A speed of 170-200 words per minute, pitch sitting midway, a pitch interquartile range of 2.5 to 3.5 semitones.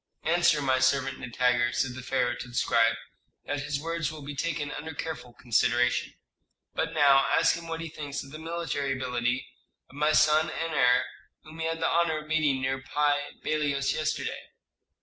Yes: average, 185 wpm; medium, 145 Hz; average, 3.2 semitones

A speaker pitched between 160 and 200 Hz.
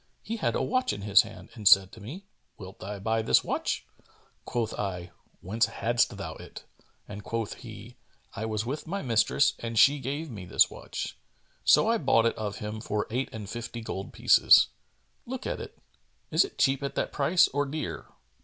No: low, 115 Hz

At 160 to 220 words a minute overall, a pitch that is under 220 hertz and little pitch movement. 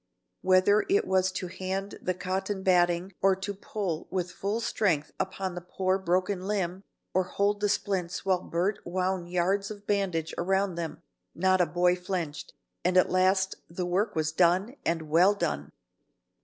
Yes: average, 165 wpm; medium, 185 Hz; narrow, 1.8 semitones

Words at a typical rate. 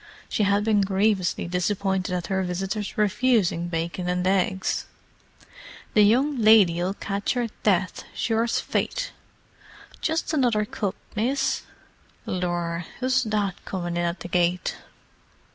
No: slow, 125 wpm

